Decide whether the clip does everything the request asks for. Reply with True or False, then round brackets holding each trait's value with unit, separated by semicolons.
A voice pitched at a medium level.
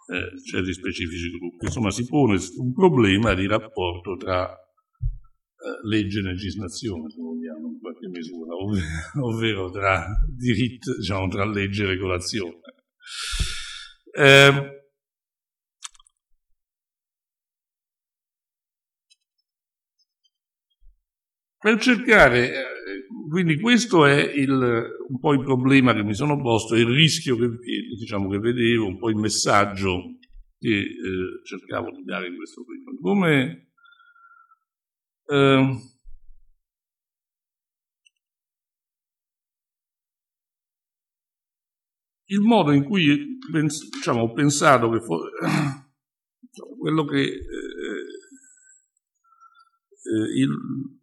False (130 Hz)